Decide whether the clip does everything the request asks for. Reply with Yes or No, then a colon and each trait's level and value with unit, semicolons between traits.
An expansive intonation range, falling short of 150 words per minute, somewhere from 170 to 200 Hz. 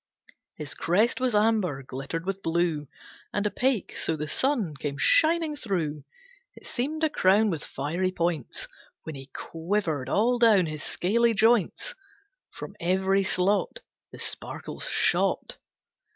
Yes: wide, 6.2 semitones; slow, 135 wpm; high, 190 Hz